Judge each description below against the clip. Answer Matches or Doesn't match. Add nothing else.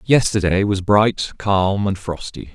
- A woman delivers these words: Doesn't match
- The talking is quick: Doesn't match